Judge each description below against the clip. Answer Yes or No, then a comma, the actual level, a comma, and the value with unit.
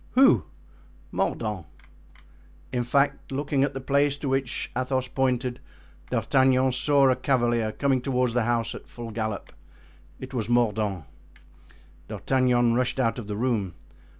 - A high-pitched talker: No, low, 125 Hz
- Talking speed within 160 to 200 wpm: No, slow, 135 wpm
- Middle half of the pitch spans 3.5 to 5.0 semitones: No, narrow, 2.4 semitones